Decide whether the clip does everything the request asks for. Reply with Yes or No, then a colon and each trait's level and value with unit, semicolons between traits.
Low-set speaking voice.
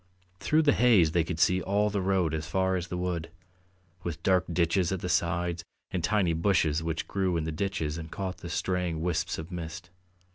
Yes: very low, 90 Hz